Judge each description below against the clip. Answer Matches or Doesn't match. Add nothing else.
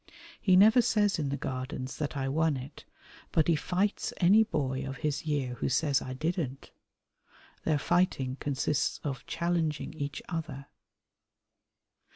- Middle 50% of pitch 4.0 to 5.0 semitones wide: Matches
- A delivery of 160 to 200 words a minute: Doesn't match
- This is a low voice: Doesn't match